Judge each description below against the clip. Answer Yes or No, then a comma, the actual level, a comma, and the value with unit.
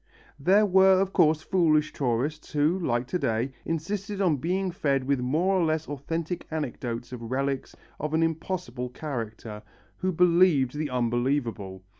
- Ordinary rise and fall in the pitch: No, wide, 5.8 semitones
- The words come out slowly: No, average, 150 wpm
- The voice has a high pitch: No, medium, 150 Hz